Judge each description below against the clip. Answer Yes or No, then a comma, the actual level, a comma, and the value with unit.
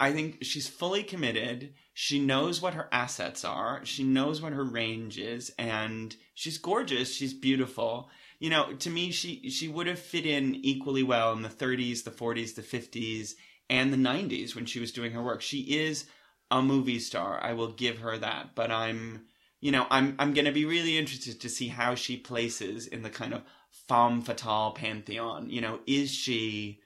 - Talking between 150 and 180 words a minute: No, average, 195 wpm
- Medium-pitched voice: No, low, 130 Hz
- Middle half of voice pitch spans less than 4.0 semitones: Yes, average, 3.5 semitones